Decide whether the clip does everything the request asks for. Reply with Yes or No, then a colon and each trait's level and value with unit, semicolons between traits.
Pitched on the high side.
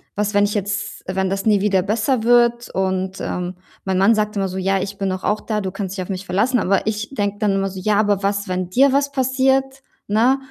Yes: high, 205 Hz